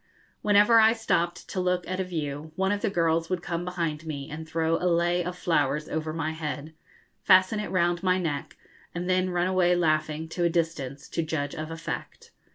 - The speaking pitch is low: No, medium, 170 Hz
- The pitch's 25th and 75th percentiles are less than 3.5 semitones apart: Yes, narrow, 2.5 semitones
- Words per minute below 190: No, average, 200 wpm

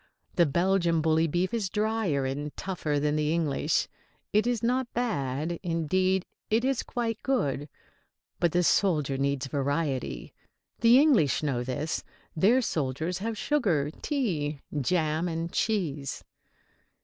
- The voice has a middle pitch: Yes, medium, 165 Hz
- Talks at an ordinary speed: No, slow, 130 wpm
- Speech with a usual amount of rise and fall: No, wide, 6.5 semitones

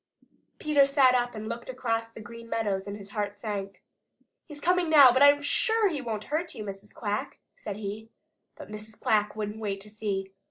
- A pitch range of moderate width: Yes, average, 4.6 semitones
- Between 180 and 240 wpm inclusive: Yes, average, 195 wpm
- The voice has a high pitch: Yes, high, 220 Hz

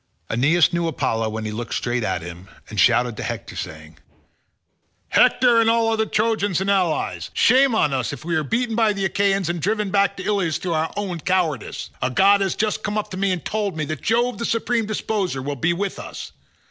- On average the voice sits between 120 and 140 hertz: No, medium, 185 Hz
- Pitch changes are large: Yes, wide, 7.5 semitones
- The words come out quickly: Yes, fast, 215 wpm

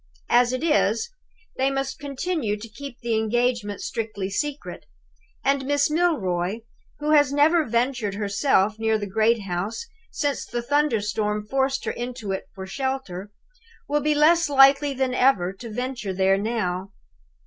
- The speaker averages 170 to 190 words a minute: No, average, 150 wpm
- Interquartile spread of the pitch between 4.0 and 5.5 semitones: Yes, average, 5.1 semitones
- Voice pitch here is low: No, high, 240 Hz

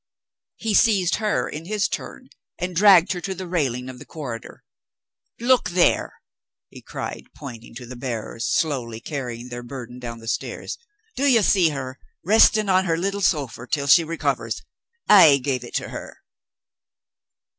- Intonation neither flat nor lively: No, wide, 7.2 semitones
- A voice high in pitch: No, medium, 155 Hz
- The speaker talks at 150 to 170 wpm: Yes, average, 160 wpm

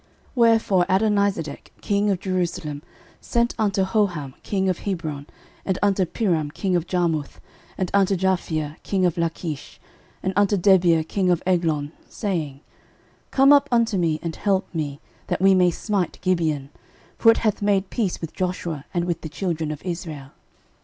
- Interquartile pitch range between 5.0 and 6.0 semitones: No, average, 3.8 semitones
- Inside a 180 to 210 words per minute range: No, average, 165 wpm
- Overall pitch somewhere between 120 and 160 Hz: No, medium, 180 Hz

